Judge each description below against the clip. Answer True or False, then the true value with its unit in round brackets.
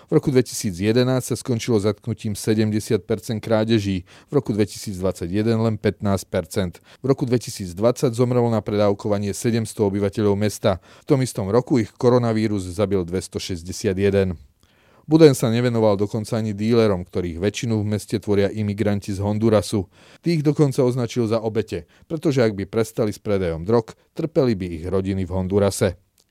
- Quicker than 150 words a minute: False (140 wpm)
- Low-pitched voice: True (110 Hz)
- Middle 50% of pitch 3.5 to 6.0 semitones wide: False (3.1 semitones)